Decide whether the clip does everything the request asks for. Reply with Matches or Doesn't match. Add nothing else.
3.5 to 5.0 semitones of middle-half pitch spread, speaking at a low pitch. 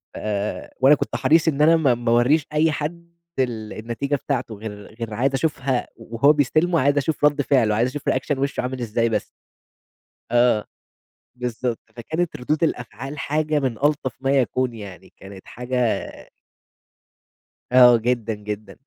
Matches